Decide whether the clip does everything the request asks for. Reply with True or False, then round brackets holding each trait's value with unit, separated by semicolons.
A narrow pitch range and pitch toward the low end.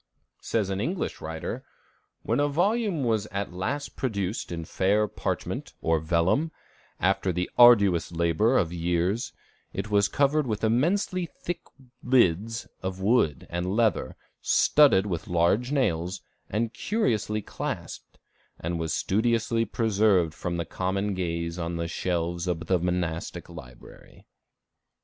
False (5.3 semitones; 95 Hz)